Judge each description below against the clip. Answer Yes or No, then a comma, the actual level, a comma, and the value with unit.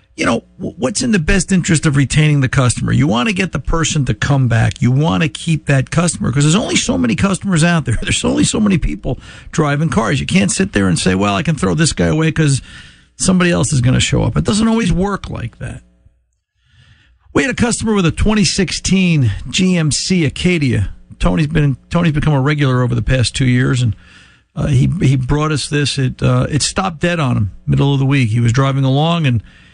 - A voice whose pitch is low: No, medium, 145 Hz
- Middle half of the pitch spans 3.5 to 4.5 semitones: No, average, 5.2 semitones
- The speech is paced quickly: Yes, fast, 225 wpm